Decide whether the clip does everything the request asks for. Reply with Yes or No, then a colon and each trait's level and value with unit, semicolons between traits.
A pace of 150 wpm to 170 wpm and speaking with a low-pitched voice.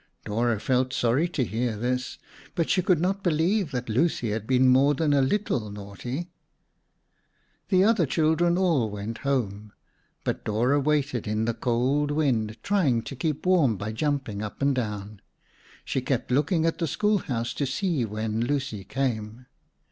Yes: average, 160 wpm; low, 130 Hz